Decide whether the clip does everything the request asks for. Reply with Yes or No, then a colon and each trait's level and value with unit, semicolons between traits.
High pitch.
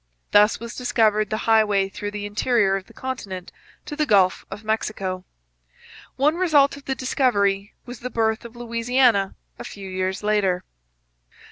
Yes: high, 215 Hz